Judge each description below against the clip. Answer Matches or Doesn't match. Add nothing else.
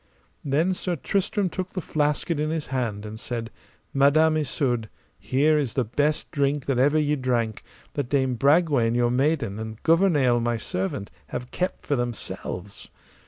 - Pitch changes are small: Doesn't match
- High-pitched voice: Doesn't match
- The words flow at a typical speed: Matches